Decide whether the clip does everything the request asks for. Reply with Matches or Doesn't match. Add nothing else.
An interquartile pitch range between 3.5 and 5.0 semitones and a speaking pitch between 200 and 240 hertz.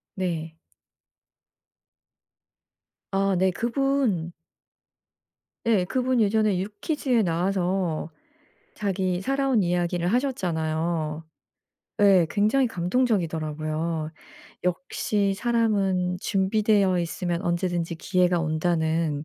Doesn't match